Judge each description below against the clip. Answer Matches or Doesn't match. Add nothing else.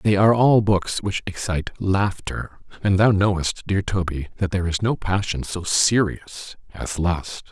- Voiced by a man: Matches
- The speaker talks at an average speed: Matches